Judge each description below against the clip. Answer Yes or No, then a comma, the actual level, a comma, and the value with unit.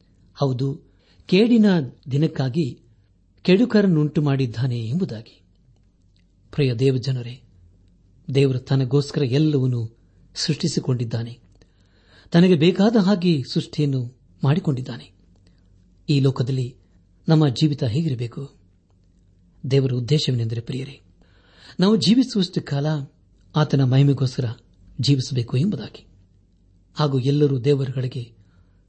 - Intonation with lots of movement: Yes, wide, 7.5 semitones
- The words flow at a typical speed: Yes, average, 75 wpm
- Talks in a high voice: No, low, 130 Hz